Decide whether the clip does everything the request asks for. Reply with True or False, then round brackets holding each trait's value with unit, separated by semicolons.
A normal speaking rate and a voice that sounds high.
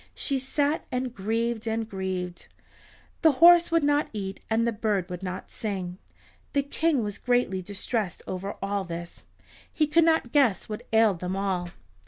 True (165 wpm; 220 Hz)